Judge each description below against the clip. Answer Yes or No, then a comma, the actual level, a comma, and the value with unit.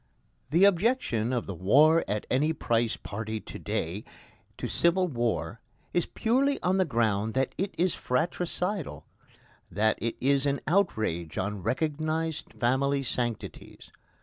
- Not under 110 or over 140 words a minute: Yes, slow, 135 wpm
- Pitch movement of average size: No, wide, 7.5 semitones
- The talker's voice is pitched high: No, low, 135 Hz